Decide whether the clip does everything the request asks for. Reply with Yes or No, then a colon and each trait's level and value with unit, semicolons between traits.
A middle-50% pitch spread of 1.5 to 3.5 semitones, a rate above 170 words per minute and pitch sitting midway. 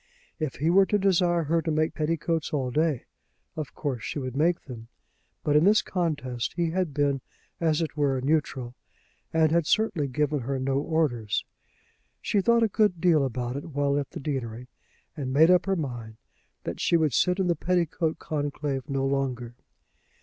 No: average, 3.9 semitones; average, 180 wpm; medium, 150 Hz